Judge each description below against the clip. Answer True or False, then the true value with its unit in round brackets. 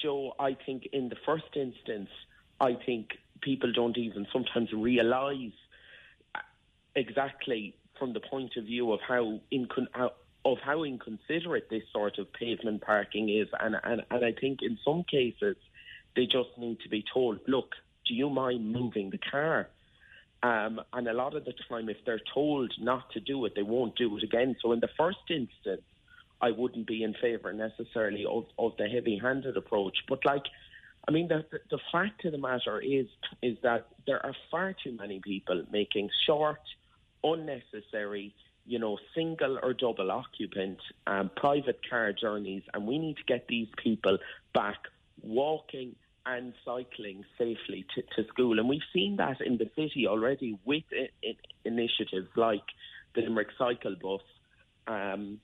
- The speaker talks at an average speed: True (165 wpm)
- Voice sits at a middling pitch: False (120 Hz)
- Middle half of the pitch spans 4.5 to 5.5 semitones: False (3.7 semitones)